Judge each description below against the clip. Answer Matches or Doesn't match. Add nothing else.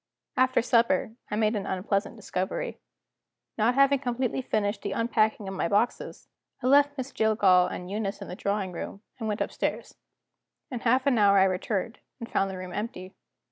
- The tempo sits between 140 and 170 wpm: Doesn't match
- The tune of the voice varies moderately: Matches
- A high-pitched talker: Matches